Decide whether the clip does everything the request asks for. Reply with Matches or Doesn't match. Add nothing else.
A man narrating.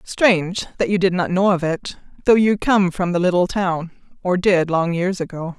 Doesn't match